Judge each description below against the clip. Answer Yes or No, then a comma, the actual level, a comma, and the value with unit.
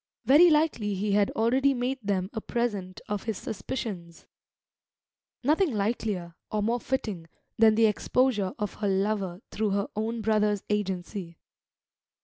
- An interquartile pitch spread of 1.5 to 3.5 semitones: Yes, average, 3.0 semitones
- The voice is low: No, high, 210 Hz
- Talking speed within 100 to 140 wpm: Yes, slow, 135 wpm